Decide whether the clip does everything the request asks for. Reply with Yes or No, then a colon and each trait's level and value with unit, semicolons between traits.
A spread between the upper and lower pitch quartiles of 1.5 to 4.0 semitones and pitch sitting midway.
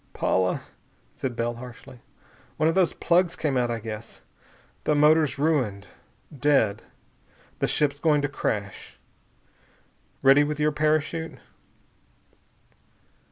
No: average, 4.5 semitones; medium, 145 Hz